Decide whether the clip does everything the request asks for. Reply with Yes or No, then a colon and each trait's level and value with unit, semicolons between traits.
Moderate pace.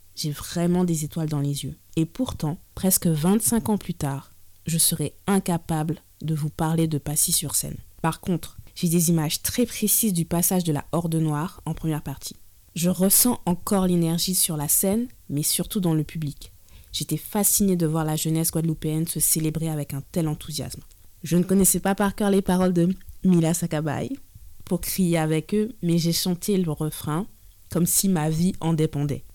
Yes: average, 185 wpm